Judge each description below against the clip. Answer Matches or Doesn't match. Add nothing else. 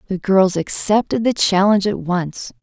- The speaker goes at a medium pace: Matches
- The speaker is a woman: Matches